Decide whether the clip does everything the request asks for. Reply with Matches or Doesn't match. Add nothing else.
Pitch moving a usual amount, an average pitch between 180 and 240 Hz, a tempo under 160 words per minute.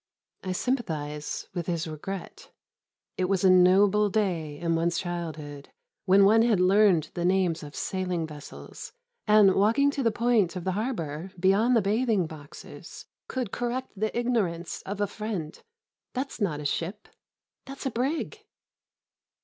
Matches